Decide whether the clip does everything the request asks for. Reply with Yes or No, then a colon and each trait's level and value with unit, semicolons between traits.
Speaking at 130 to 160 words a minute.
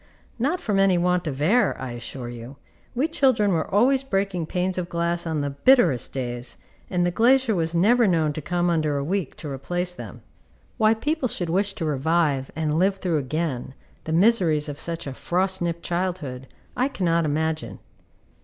No: average, 180 wpm